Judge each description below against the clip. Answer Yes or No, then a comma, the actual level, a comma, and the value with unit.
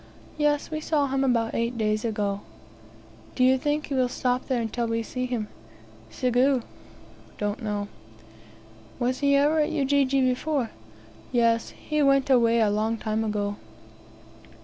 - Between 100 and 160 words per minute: Yes, average, 150 wpm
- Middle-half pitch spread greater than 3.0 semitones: Yes, average, 3.6 semitones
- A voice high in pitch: Yes, very high, 250 Hz